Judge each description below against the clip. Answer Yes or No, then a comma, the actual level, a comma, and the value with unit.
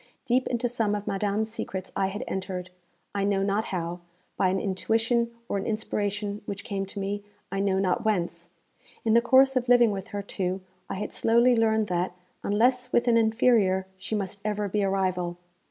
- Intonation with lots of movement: No, average, 2.8 semitones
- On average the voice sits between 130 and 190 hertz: No, high, 205 Hz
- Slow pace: No, average, 190 wpm